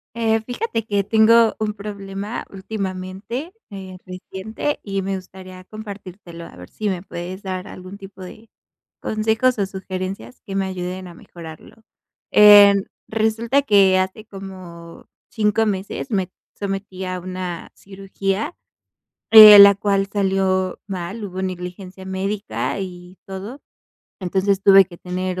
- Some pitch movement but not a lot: No, narrow, 2.1 semitones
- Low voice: No, high, 195 Hz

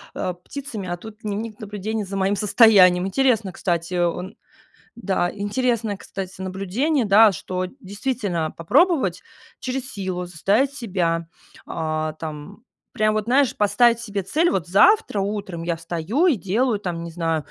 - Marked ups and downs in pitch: No, average, 4.4 semitones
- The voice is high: Yes, high, 200 Hz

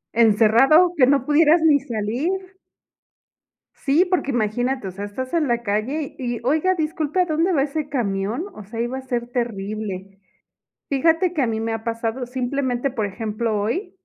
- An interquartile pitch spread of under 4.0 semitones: No, wide, 5.4 semitones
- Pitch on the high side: Yes, very high, 250 Hz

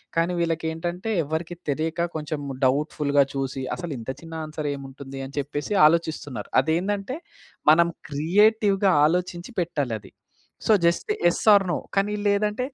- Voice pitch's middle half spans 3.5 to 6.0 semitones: Yes, average, 4.0 semitones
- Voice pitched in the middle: Yes, medium, 165 Hz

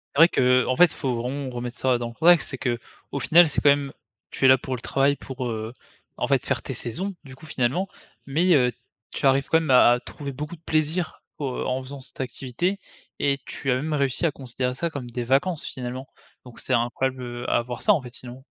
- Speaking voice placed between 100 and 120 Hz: No, low, 130 Hz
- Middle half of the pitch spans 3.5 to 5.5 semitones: No, average, 3.1 semitones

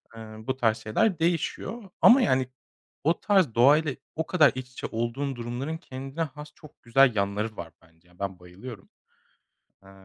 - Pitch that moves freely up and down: Yes, wide, 5.8 semitones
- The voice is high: No, low, 130 Hz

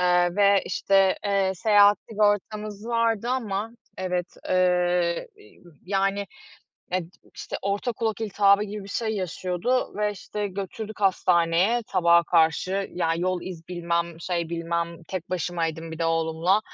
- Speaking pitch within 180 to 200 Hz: Yes, medium, 185 Hz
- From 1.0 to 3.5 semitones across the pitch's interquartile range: Yes, average, 3.1 semitones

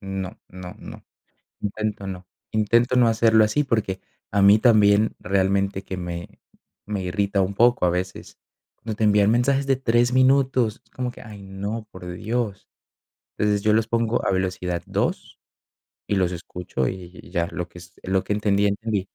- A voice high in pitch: No, low, 100 Hz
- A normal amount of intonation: Yes, average, 3.2 semitones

